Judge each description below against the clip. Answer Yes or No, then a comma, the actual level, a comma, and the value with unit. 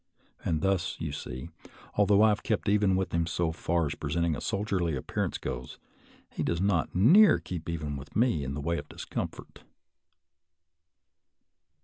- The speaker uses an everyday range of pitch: Yes, average, 4.4 semitones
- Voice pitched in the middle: No, very low, 85 Hz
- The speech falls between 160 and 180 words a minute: Yes, average, 165 wpm